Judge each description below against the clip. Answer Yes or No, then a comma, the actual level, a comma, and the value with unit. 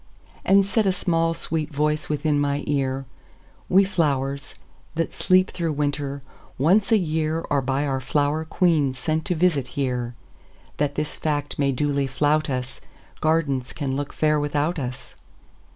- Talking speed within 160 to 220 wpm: No, slow, 135 wpm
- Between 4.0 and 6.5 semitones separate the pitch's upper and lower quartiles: No, average, 2.8 semitones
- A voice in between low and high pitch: Yes, medium, 145 Hz